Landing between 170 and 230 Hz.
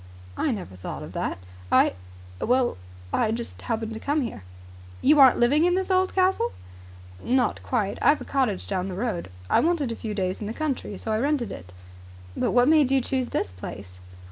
No: high, 240 Hz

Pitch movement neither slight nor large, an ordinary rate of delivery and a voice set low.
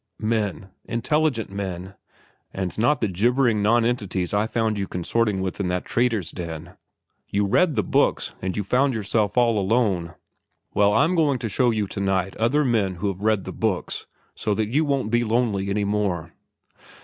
Yes: average, 3.5 semitones; average, 175 wpm; low, 105 Hz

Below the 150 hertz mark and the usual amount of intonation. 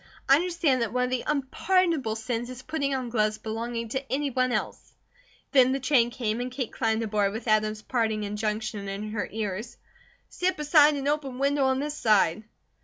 No: high, 245 Hz; average, 4.1 semitones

